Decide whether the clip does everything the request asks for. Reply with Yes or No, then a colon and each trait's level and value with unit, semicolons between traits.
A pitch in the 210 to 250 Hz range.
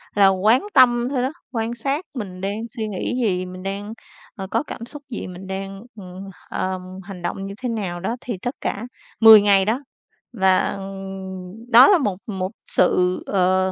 No: high, 200 Hz